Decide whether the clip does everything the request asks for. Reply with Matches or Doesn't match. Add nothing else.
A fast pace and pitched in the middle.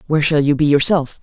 Matches